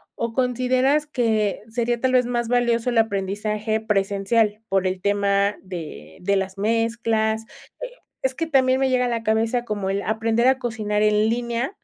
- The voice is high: Yes, high, 225 Hz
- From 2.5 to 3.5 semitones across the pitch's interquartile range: Yes, average, 3.0 semitones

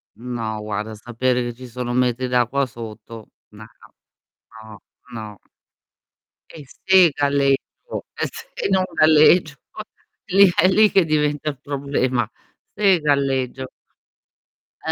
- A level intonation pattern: No, average, 4.2 semitones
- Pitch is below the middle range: Yes, low, 130 Hz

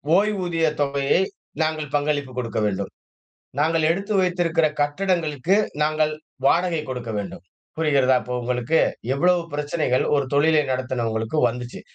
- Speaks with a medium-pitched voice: Yes, medium, 150 Hz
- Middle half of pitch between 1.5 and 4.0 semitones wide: No, average, 4.4 semitones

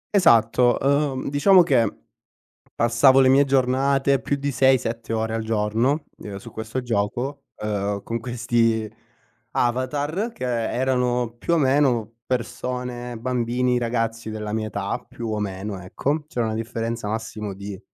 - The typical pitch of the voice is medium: No, low, 120 Hz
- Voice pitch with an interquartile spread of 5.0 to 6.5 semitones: No, average, 2.9 semitones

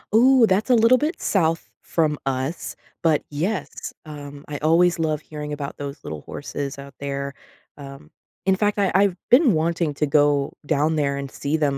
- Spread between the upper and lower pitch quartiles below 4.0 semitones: No, average, 4.3 semitones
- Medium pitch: Yes, medium, 155 Hz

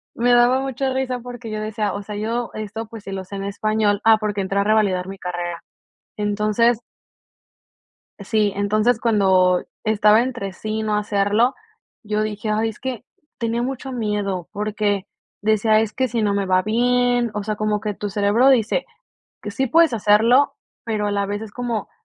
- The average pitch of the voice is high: Yes, high, 215 Hz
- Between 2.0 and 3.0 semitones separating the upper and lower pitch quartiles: Yes, narrow, 2.5 semitones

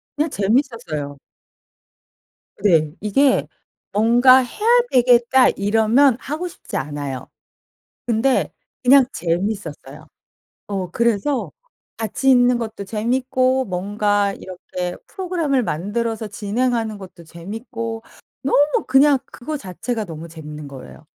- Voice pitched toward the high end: Yes, high, 225 Hz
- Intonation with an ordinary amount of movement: No, wide, 5.8 semitones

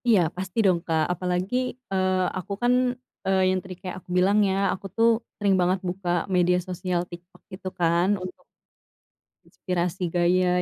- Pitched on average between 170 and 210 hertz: Yes, medium, 185 Hz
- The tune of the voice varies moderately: No, narrow, 1.1 semitones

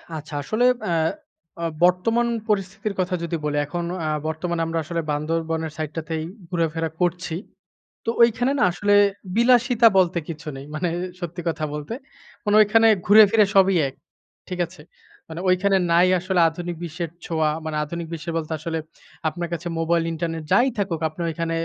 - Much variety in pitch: No, average, 3.2 semitones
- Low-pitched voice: No, medium, 170 Hz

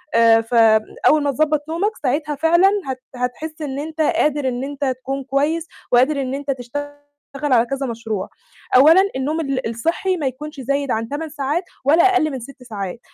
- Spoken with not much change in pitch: No, average, 3.5 semitones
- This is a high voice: Yes, very high, 275 Hz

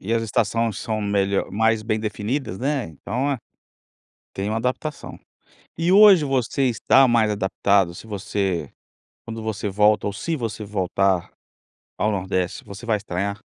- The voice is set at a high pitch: No, low, 110 Hz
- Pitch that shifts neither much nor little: Yes, average, 3.2 semitones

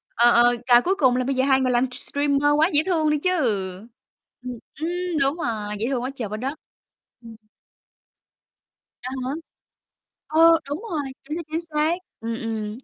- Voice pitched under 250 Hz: No, very high, 270 Hz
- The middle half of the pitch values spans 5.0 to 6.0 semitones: No, average, 4.6 semitones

